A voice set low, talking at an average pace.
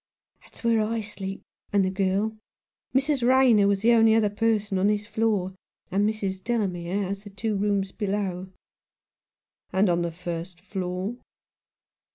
No: high, 205 Hz; average, 150 wpm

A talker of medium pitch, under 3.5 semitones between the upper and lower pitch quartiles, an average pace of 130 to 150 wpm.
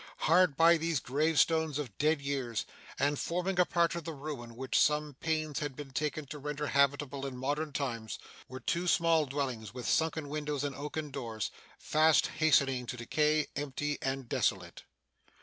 No: medium, 145 Hz; average, 2.7 semitones; average, 165 wpm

